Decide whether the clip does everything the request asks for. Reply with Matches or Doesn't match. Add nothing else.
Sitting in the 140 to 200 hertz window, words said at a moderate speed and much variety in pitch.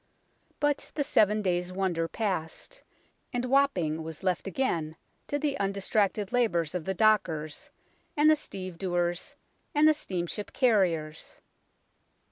Doesn't match